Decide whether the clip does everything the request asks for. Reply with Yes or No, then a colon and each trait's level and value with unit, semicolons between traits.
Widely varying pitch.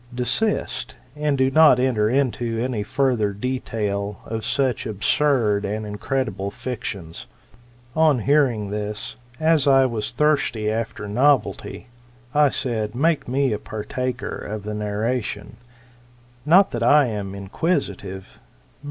No: average, 4.3 semitones